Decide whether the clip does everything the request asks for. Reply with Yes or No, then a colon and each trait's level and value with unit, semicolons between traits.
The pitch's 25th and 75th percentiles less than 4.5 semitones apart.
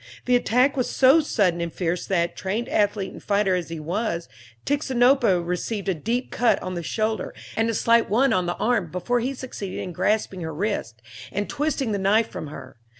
No: wide, 5.4 semitones